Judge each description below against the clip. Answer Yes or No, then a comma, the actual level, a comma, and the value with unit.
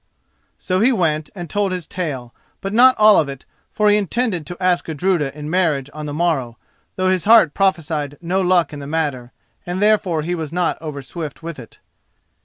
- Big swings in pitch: No, average, 4.1 semitones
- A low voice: No, medium, 170 Hz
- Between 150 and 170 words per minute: No, average, 195 wpm